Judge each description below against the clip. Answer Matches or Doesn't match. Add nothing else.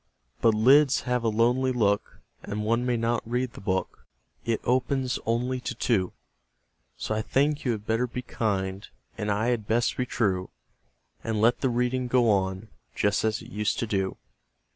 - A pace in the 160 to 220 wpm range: Matches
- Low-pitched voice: Matches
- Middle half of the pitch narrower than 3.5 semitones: Matches